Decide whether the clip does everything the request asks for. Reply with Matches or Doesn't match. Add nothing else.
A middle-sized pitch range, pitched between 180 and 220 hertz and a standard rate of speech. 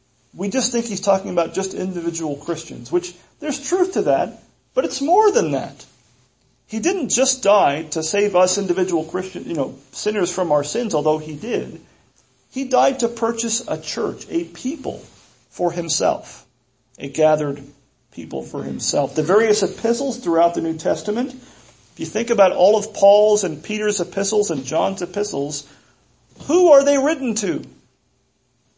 Doesn't match